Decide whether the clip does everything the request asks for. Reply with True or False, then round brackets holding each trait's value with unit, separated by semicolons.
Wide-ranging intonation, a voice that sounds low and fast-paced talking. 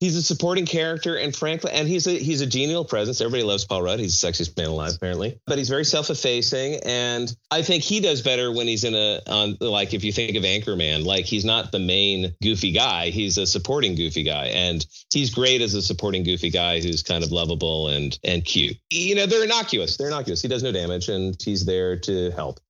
True (7.7 semitones; 105 Hz; 225 wpm)